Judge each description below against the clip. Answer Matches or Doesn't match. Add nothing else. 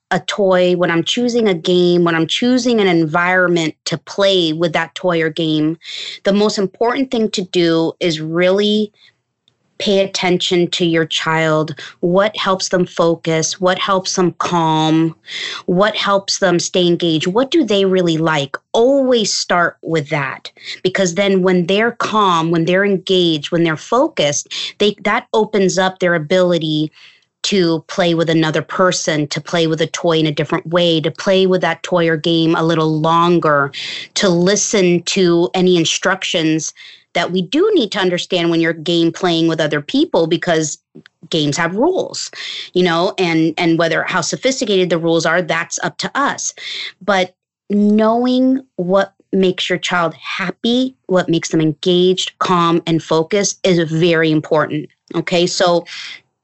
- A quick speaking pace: Doesn't match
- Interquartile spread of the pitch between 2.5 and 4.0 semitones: Matches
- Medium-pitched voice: Matches